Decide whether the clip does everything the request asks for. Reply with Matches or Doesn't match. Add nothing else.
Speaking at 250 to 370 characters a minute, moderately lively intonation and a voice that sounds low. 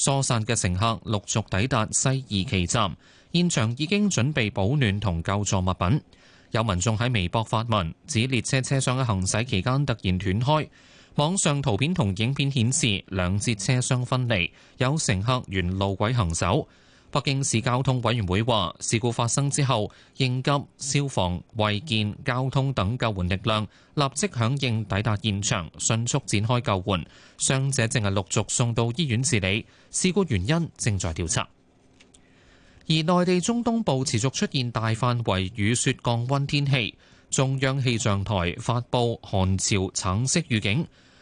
Doesn't match